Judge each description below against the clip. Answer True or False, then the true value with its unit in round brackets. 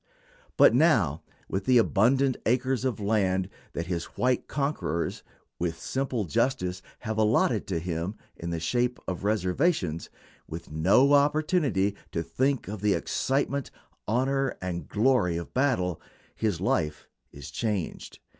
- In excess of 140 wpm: False (135 wpm)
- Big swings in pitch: True (6.5 semitones)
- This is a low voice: True (105 Hz)